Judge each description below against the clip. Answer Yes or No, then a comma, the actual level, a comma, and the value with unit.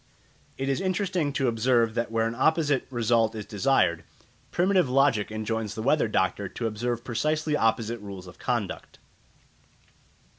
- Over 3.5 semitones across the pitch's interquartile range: Yes, average, 4.3 semitones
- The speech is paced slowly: No, average, 145 wpm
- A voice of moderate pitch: No, low, 120 Hz